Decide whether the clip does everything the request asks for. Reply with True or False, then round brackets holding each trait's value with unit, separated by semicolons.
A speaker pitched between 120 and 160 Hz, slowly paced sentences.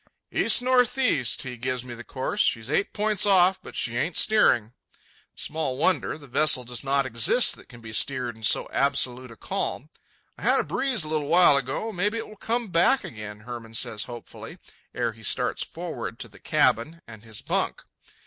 False (135 Hz; 185 wpm)